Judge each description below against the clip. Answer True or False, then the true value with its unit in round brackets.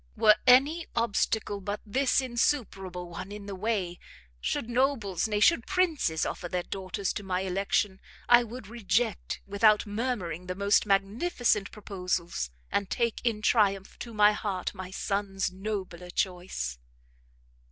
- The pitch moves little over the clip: False (3.7 semitones)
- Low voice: False (200 Hz)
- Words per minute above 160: False (140 wpm)